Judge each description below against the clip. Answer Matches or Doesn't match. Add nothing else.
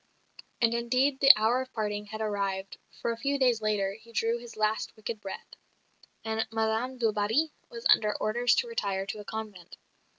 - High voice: Matches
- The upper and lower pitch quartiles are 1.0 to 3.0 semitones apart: Matches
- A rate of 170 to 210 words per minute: Matches